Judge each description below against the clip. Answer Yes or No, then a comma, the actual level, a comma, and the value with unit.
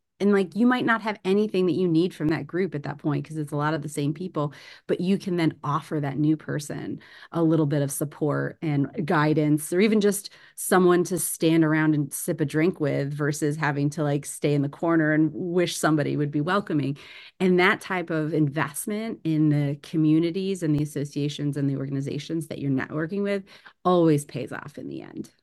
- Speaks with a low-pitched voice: No, medium, 155 Hz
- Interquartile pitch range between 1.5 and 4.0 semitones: Yes, average, 3.4 semitones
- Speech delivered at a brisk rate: Yes, fast, 210 wpm